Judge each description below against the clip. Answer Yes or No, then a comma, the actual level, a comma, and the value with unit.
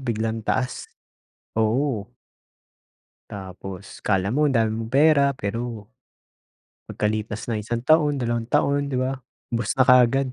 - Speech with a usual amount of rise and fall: Yes, average, 3.6 semitones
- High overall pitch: No, low, 120 Hz